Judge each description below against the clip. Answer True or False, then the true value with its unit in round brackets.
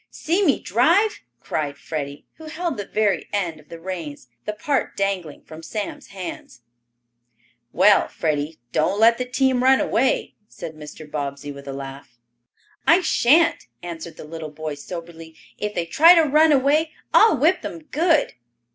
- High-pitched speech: True (195 Hz)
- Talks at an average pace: True (160 wpm)